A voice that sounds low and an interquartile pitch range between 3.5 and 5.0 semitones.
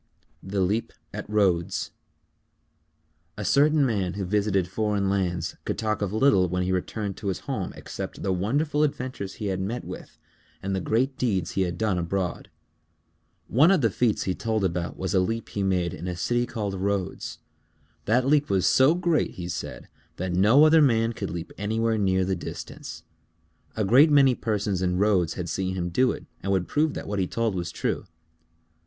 Yes: low, 100 Hz; average, 3.9 semitones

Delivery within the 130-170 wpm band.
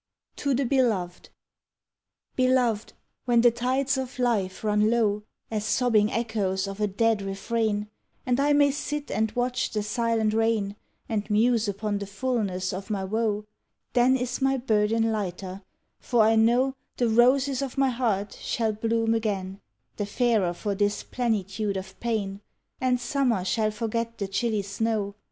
Yes: average, 155 wpm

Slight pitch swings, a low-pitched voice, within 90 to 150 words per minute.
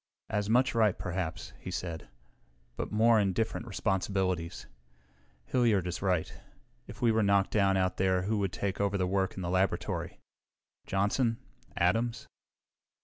No: average, 3.0 semitones; low, 100 Hz; average, 145 wpm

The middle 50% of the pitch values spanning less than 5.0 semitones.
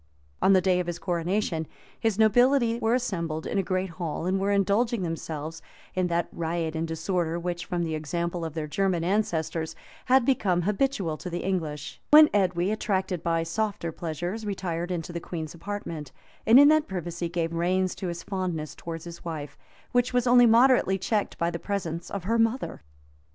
Yes: average, 3.7 semitones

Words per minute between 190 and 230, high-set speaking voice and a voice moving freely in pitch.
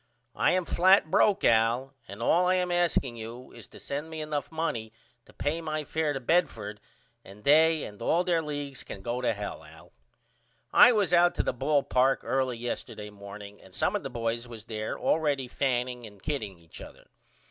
No: average, 195 wpm; low, 135 Hz; wide, 5.9 semitones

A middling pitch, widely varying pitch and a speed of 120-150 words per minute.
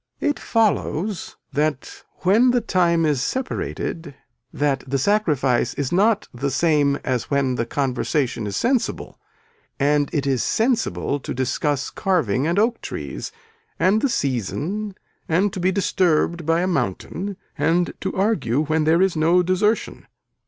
Yes: medium, 165 Hz; wide, 5.7 semitones; average, 145 wpm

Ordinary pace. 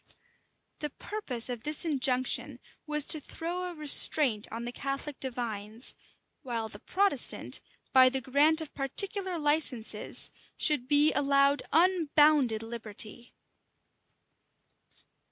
No: slow, 110 wpm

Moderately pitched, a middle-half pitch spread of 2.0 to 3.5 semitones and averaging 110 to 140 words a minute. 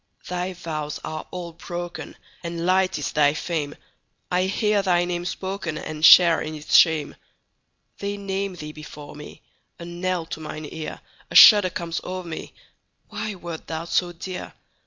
Yes: medium, 175 Hz; average, 2.8 semitones; slow, 135 wpm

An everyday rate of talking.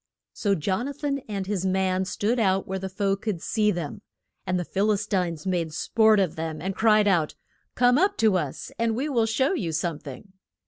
No: fast, 215 wpm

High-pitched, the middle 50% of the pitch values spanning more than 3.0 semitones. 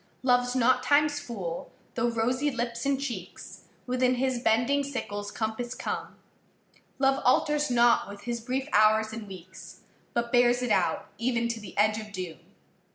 No: high, 240 Hz; average, 2.7 semitones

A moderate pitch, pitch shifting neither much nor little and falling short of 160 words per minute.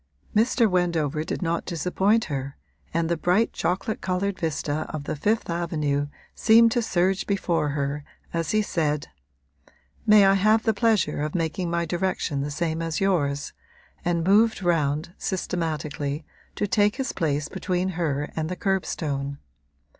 Yes: medium, 170 Hz; average, 4.3 semitones; average, 150 wpm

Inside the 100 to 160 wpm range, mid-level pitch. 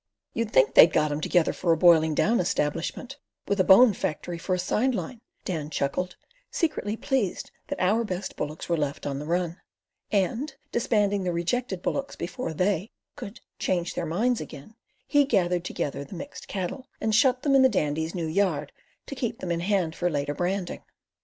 No: average, 185 wpm; medium, 180 Hz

